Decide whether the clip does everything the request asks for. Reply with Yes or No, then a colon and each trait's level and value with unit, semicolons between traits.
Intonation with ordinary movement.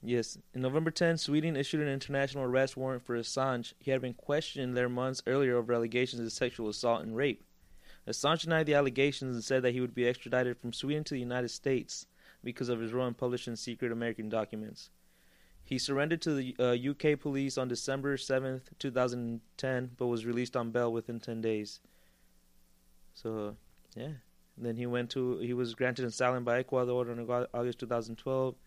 No: narrow, 2.1 semitones